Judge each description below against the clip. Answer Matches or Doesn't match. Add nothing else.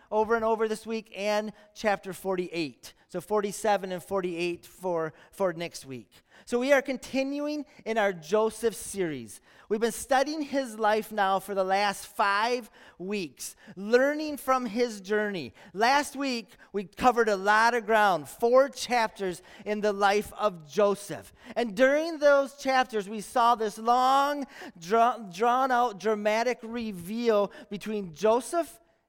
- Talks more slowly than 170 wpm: Matches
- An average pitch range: Matches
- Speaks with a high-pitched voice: Matches